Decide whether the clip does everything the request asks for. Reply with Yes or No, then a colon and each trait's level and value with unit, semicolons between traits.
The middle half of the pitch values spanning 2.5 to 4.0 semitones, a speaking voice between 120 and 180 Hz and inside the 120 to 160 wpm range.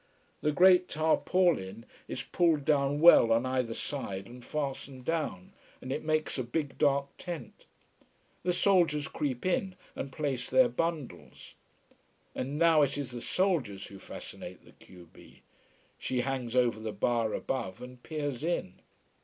No: average, 4.8 semitones; medium, 140 Hz; average, 150 wpm